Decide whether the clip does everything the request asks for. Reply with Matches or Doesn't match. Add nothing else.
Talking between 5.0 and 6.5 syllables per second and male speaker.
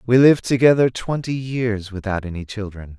Matches